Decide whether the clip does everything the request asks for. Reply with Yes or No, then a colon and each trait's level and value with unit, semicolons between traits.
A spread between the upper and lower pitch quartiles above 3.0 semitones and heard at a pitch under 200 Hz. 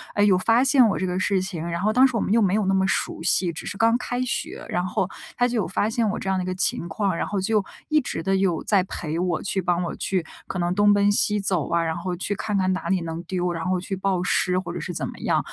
No: narrow, 2.6 semitones; high, 190 Hz